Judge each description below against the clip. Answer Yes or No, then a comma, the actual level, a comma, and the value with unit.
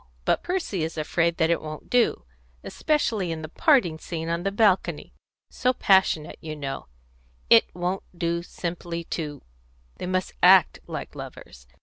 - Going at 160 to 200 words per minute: No, average, 150 wpm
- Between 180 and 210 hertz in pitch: No, medium, 170 Hz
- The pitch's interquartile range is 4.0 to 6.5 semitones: No, average, 3.3 semitones